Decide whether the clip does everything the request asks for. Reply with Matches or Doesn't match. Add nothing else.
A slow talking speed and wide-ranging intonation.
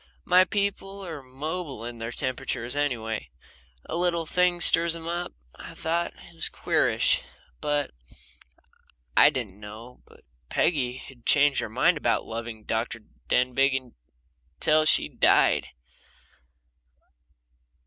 Matches